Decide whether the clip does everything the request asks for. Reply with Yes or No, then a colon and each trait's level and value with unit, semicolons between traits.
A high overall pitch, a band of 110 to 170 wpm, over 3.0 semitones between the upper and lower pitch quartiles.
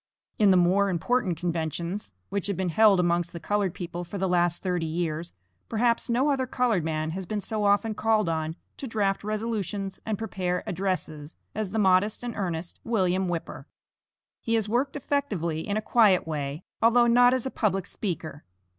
No: high, 195 Hz; average, 180 wpm; average, 4.2 semitones